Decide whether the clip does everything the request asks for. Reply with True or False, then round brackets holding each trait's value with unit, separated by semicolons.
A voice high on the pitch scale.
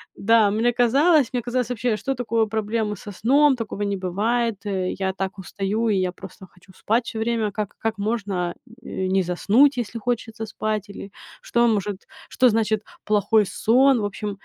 True (220 Hz)